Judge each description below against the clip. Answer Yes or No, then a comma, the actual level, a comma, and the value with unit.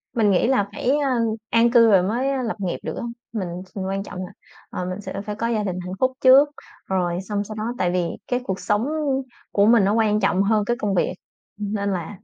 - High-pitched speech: Yes, high, 210 Hz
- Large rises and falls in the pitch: No, average, 3.4 semitones